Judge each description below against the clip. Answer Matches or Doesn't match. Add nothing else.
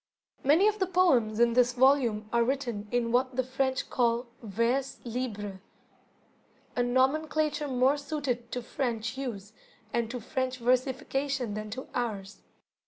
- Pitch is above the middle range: Matches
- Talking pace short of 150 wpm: Matches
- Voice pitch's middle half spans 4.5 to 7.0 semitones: Doesn't match